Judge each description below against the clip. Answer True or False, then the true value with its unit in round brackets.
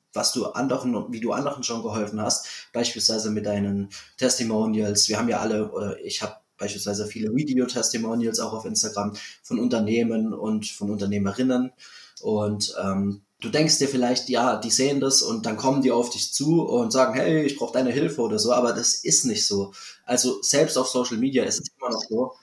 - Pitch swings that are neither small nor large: True (3.6 semitones)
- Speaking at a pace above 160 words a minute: True (190 wpm)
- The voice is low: True (115 Hz)